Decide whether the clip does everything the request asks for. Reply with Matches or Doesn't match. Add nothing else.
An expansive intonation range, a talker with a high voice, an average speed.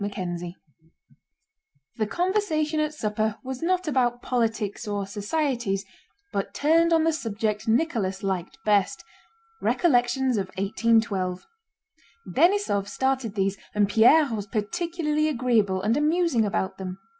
Doesn't match